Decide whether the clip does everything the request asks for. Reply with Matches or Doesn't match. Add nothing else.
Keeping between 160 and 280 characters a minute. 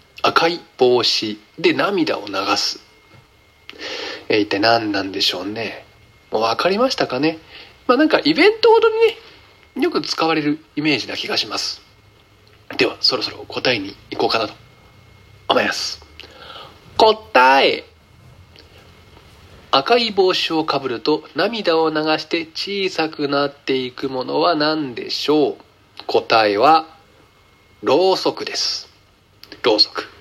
Matches